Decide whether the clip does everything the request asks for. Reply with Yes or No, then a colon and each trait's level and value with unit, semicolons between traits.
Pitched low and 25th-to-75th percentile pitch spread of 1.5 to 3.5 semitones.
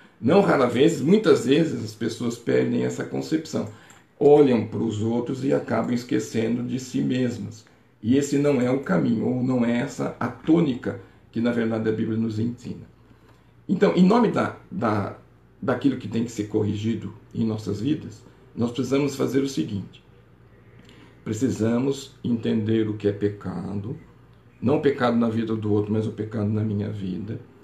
Yes: low, 115 Hz; average, 3.0 semitones